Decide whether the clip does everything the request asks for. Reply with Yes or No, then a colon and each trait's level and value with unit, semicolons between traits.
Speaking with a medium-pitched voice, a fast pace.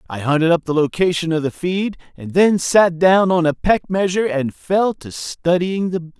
Yes: medium, 170 Hz; fast, 215 wpm